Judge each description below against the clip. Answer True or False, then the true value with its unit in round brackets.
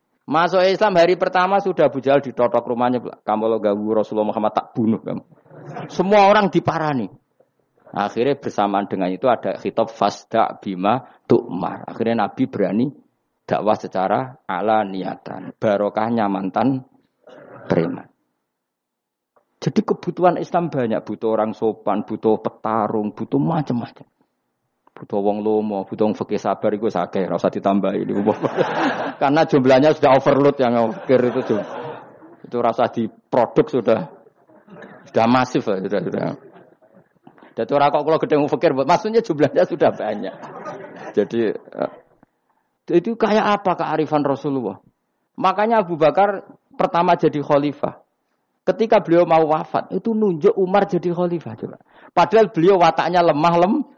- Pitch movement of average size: False (7.9 semitones)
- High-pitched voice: False (140 Hz)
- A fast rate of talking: False (125 wpm)